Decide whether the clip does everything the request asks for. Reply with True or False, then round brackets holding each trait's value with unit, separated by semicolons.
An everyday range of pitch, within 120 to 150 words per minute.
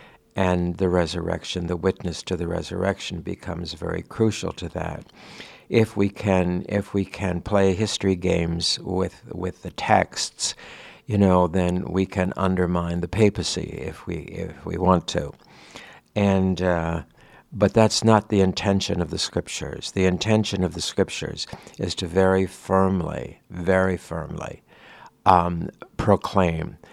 False (2.1 semitones; 140 wpm)